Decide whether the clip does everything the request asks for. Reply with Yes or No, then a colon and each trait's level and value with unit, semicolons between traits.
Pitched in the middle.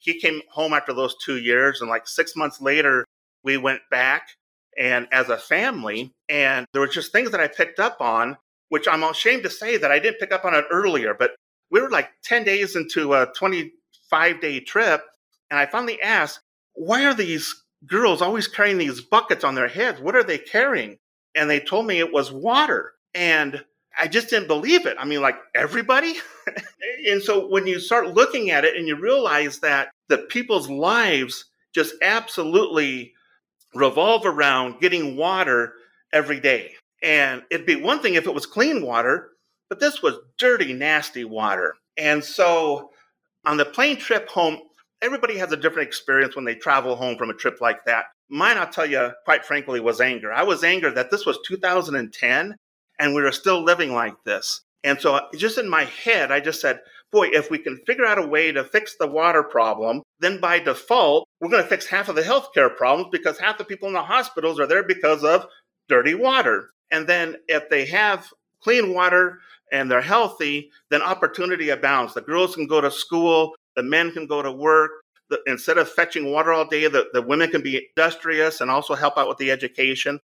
Yes: medium, 160 Hz